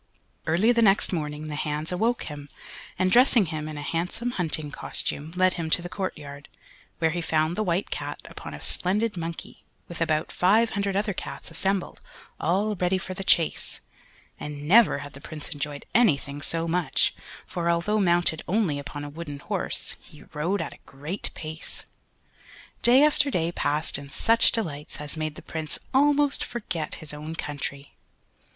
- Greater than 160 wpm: Yes, average, 170 wpm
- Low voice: No, medium, 165 Hz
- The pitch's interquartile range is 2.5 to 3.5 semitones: No, average, 4.6 semitones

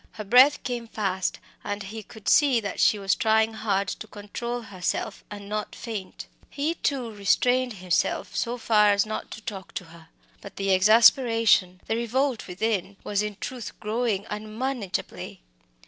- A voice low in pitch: No, high, 215 Hz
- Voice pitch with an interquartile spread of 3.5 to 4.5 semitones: No, average, 2.9 semitones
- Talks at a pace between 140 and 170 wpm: Yes, average, 165 wpm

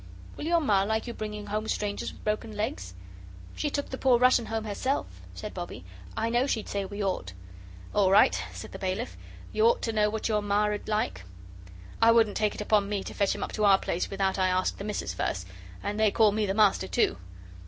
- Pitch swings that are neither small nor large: No, narrow, 2.1 semitones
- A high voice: Yes, high, 210 Hz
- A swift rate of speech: Yes, fast, 225 wpm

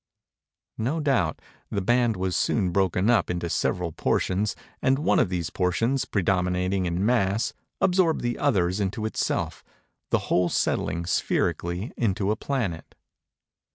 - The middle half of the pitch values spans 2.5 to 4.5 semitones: No, average, 4.9 semitones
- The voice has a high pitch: No, very low, 95 Hz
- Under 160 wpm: Yes, slow, 135 wpm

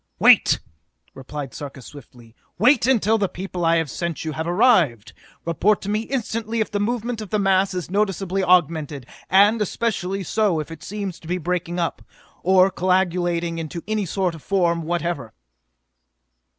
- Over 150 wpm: Yes, average, 165 wpm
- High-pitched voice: No, medium, 180 Hz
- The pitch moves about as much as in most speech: Yes, average, 3.8 semitones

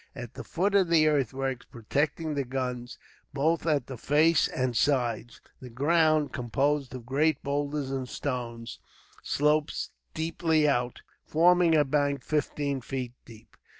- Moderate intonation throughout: Yes, average, 3.5 semitones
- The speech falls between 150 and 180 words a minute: No, average, 140 wpm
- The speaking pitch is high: No, medium, 140 Hz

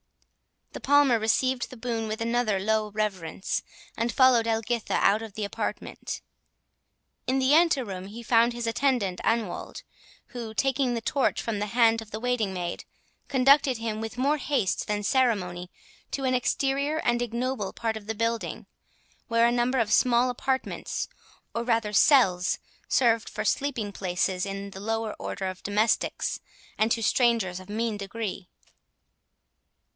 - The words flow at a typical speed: Yes, average, 150 wpm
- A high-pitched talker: Yes, high, 230 Hz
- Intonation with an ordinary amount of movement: Yes, average, 3.1 semitones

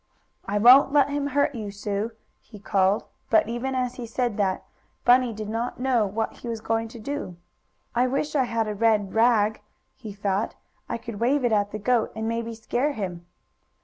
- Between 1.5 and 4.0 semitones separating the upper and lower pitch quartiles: Yes, average, 3.1 semitones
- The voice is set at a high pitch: Yes, high, 230 Hz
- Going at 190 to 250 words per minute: Yes, average, 195 wpm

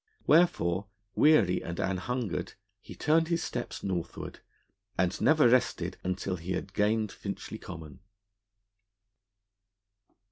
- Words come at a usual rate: No, slow, 110 wpm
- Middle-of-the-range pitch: No, low, 100 Hz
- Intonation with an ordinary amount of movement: No, wide, 5.8 semitones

